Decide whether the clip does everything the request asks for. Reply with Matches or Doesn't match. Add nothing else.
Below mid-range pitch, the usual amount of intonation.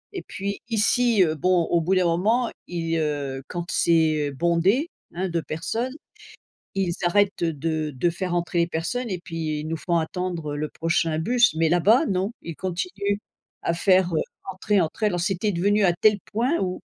Doesn't match